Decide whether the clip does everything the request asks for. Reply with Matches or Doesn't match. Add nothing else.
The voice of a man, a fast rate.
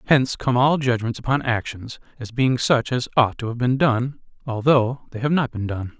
Matches